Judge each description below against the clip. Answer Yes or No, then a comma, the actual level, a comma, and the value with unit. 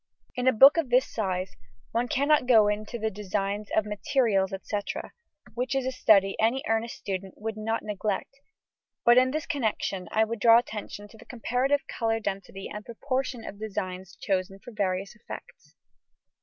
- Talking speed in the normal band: Yes, average, 170 wpm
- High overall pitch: Yes, high, 220 Hz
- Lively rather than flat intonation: No, average, 3.7 semitones